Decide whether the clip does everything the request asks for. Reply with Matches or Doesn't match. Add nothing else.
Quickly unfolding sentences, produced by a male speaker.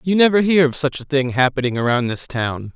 Matches